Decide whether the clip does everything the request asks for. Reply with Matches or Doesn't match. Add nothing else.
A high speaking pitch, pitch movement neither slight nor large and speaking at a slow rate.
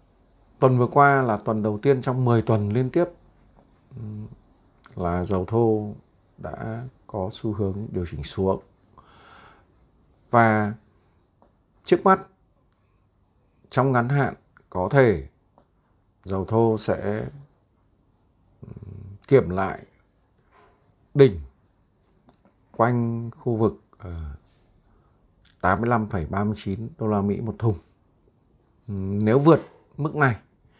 Doesn't match